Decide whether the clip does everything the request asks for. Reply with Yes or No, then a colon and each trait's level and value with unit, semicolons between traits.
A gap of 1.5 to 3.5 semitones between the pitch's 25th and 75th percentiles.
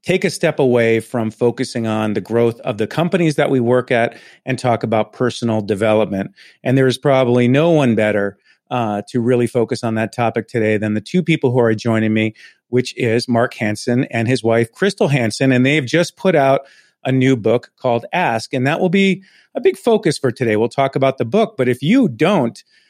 No: average, 4.2 semitones